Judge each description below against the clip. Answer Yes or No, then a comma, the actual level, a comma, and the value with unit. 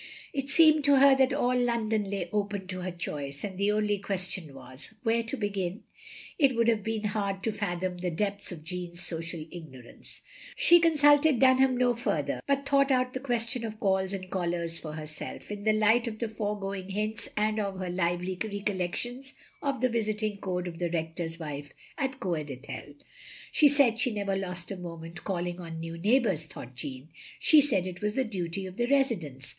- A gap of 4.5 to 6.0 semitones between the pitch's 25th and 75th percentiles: Yes, average, 5.2 semitones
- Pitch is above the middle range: Yes, high, 200 Hz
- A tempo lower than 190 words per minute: No, average, 195 wpm